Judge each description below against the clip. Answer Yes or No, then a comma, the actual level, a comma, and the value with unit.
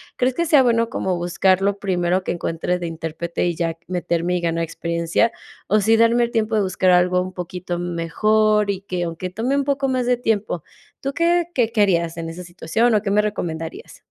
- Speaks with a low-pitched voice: No, medium, 185 Hz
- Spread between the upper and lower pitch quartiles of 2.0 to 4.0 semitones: No, average, 4.7 semitones